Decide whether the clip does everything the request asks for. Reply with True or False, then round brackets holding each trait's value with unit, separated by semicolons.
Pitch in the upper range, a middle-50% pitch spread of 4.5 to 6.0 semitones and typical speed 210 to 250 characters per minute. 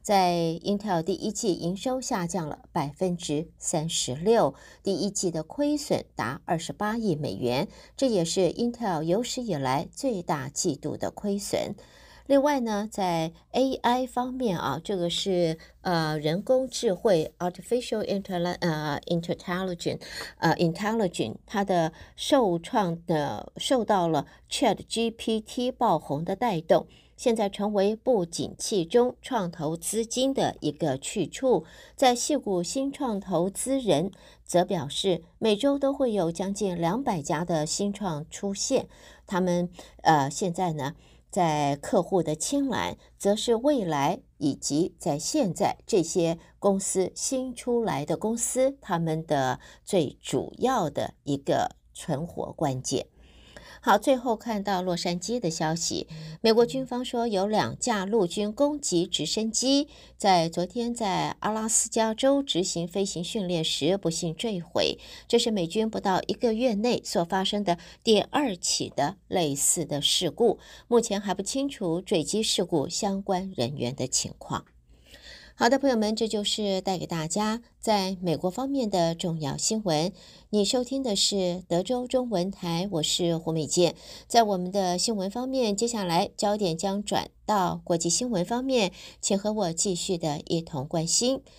True (195 Hz; 5.3 semitones; 240 characters per minute)